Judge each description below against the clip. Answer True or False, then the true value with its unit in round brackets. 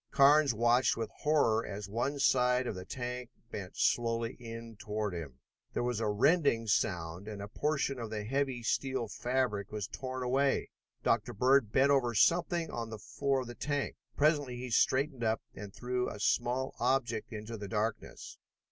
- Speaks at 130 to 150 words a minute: False (175 wpm)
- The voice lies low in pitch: True (120 Hz)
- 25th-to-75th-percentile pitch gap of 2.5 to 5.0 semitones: True (3.6 semitones)